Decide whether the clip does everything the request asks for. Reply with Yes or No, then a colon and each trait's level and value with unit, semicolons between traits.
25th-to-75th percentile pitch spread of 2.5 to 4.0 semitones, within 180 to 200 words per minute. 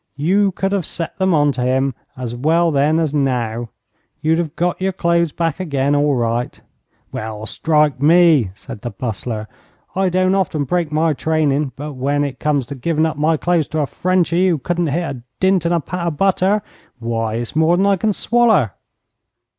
No: average, 4.6 semitones; average, 195 wpm